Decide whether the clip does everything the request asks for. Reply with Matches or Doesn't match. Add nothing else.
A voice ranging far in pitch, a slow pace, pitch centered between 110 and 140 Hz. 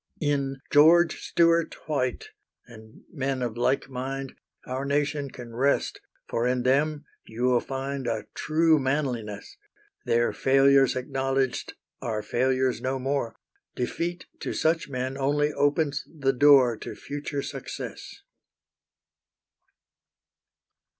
Doesn't match